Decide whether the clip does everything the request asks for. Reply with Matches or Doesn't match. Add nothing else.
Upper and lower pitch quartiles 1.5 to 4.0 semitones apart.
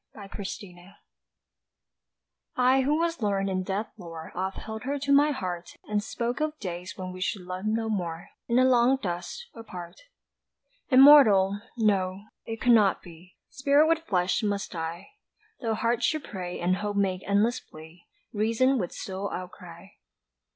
Doesn't match